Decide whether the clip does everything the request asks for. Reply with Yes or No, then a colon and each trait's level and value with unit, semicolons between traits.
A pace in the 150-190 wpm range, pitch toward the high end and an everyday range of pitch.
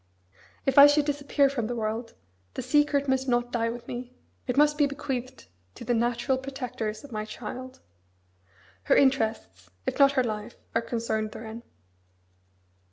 Yes: average, 160 wpm; high, 245 Hz; average, 3.3 semitones